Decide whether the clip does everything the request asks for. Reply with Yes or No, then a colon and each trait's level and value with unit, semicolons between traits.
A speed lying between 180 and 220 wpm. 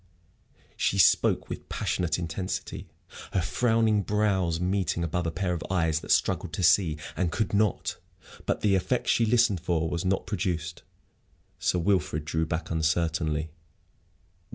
No: average, 145 wpm